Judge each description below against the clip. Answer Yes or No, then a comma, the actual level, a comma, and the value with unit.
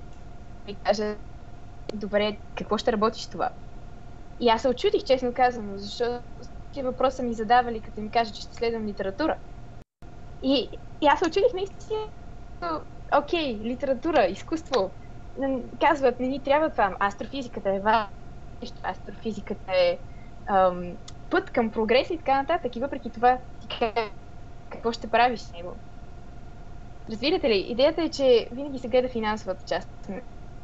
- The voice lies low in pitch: No, high, 245 Hz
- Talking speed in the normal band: Yes, average, 135 wpm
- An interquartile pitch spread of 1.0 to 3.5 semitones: No, average, 4.3 semitones